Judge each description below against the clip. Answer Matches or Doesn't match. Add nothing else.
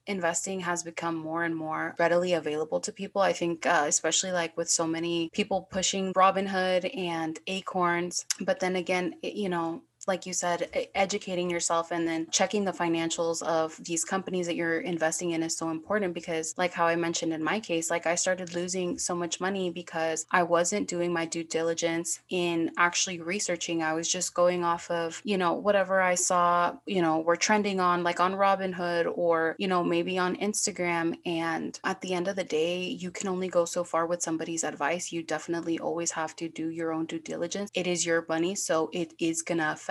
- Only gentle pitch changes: Matches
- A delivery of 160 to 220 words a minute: Matches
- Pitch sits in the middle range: Matches